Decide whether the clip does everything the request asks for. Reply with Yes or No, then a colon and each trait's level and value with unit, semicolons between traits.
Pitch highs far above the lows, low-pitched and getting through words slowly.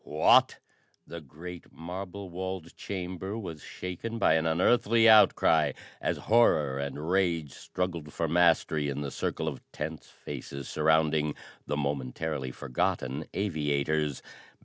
No: average, 3.8 semitones; very low, 80 Hz; slow, 125 wpm